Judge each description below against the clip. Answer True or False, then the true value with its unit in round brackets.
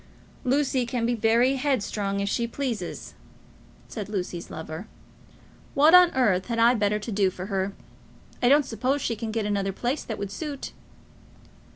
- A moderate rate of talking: True (160 wpm)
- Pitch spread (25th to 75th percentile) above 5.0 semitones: False (4.5 semitones)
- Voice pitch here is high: True (230 Hz)